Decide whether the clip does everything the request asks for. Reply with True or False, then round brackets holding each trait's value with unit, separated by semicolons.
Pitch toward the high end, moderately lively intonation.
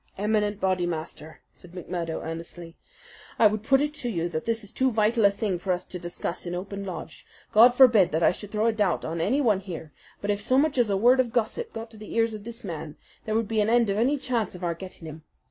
True (205 Hz; 4.5 semitones)